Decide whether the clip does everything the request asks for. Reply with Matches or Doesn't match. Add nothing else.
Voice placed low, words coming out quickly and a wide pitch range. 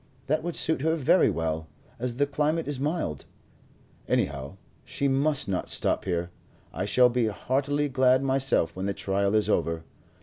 Doesn't match